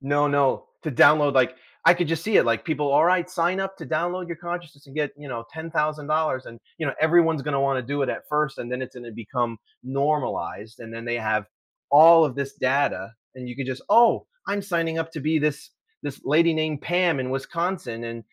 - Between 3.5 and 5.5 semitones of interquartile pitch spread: Yes, average, 4.2 semitones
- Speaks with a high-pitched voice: No, medium, 145 Hz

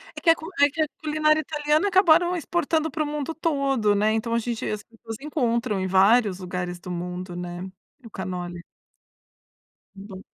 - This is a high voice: Yes, high, 235 Hz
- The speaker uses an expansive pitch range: Yes, wide, 8.5 semitones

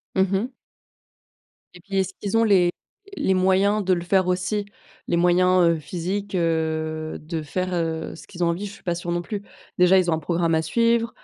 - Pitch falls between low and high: Yes, medium, 180 Hz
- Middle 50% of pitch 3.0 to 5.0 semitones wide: No, narrow, 2.5 semitones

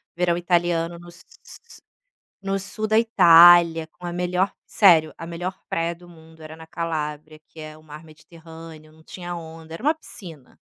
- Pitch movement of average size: No, narrow, 1.6 semitones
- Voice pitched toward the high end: No, medium, 170 Hz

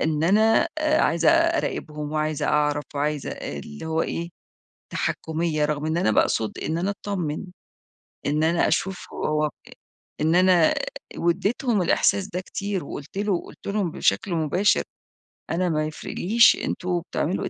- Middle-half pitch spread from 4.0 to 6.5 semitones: Yes, average, 4.3 semitones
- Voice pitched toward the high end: No, medium, 170 Hz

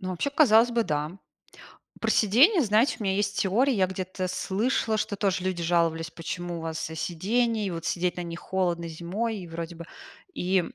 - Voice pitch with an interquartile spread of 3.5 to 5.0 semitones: Yes, average, 4.2 semitones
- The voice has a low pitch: No, medium, 185 Hz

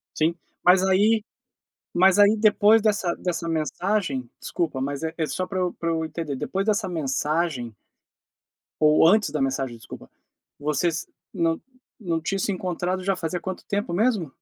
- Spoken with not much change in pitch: No, average, 3.9 semitones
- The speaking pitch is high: No, medium, 175 Hz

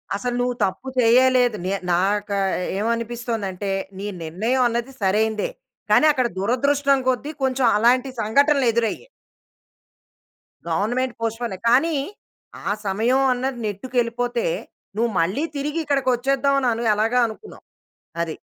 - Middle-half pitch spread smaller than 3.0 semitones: No, average, 3.6 semitones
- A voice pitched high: Yes, high, 240 Hz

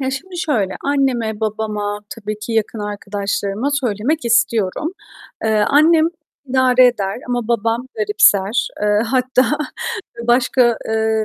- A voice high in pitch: Yes, high, 225 Hz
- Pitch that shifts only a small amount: No, average, 3.5 semitones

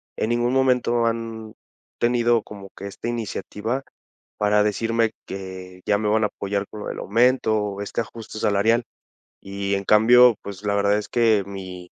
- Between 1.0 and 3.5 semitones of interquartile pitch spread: Yes, average, 2.7 semitones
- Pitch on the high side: No, low, 105 Hz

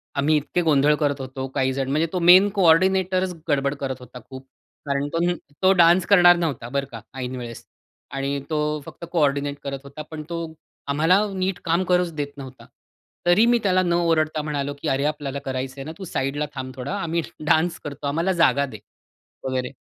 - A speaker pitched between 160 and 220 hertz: No, medium, 150 Hz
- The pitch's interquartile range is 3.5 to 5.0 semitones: Yes, average, 3.9 semitones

